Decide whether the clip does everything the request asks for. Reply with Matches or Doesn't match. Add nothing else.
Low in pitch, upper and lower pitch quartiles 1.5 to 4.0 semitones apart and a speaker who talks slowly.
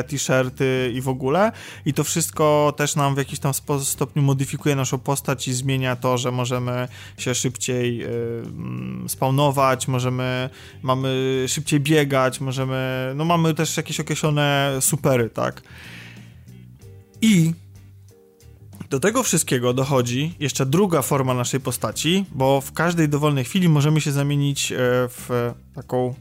Doesn't match